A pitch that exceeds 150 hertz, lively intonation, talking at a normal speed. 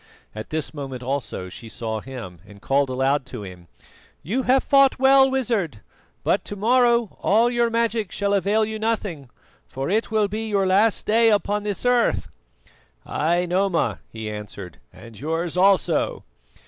Yes: high, 190 Hz; wide, 9.0 semitones; average, 160 wpm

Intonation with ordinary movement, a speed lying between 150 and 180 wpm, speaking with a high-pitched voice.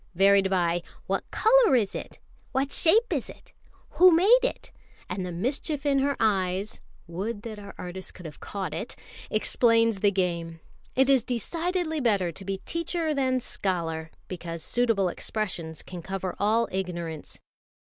No: wide, 6.9 semitones; average, 155 wpm; high, 205 Hz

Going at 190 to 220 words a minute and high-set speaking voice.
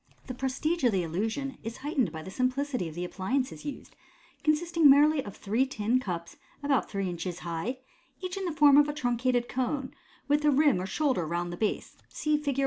Yes: average, 200 wpm; very high, 255 Hz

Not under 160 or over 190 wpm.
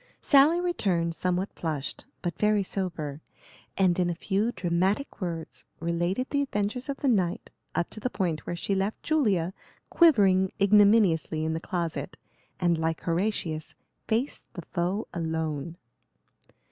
No: average, 140 wpm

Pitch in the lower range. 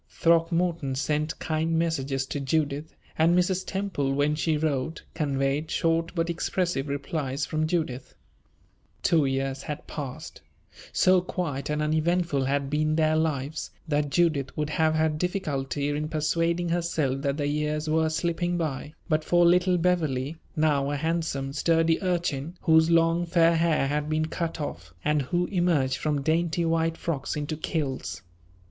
No: medium, 155 Hz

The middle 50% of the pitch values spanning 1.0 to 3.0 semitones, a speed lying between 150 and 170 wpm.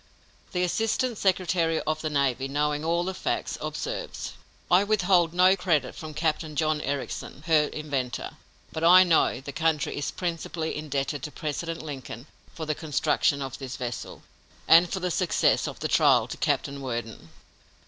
No: average, 3.7 semitones; average, 160 wpm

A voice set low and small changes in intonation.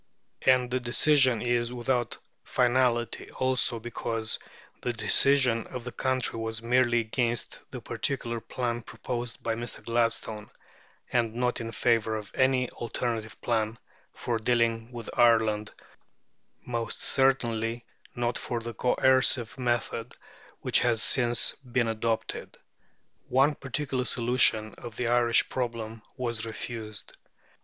Yes: low, 120 Hz; narrow, 1.6 semitones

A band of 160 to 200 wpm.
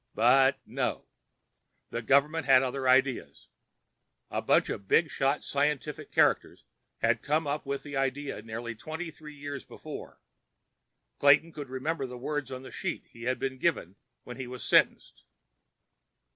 No: average, 145 wpm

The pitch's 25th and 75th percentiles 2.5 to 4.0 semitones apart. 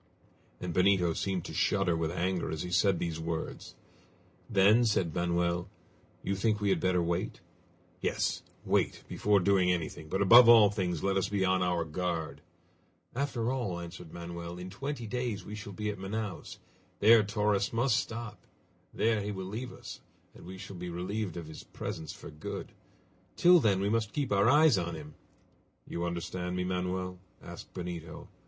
Yes: average, 3.4 semitones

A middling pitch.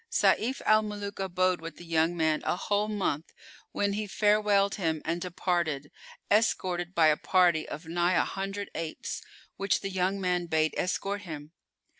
Yes: medium, 180 Hz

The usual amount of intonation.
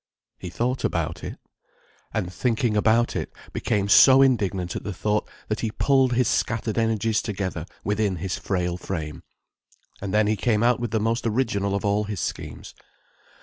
Yes: average, 3.1 semitones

